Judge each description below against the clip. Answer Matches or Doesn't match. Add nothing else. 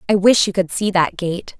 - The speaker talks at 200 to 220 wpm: Doesn't match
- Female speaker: Matches